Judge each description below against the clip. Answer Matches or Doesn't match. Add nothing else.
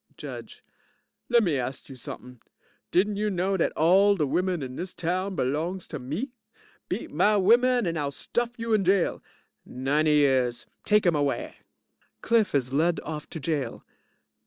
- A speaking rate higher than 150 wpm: Matches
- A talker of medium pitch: Matches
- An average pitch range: Doesn't match